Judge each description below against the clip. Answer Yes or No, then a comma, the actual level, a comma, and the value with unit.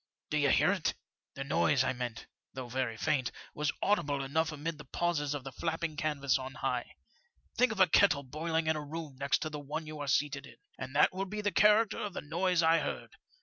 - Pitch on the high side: No, medium, 150 Hz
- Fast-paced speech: Yes, fast, 235 wpm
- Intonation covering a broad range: No, average, 3.2 semitones